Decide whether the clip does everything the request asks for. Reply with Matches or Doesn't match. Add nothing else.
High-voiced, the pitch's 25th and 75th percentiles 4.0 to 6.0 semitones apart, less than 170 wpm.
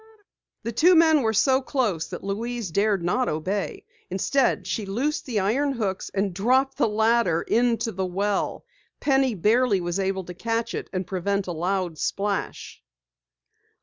Matches